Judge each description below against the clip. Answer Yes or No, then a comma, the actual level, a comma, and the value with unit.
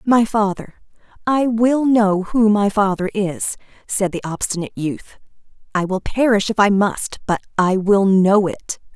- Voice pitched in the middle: No, high, 205 Hz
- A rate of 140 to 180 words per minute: Yes, average, 155 wpm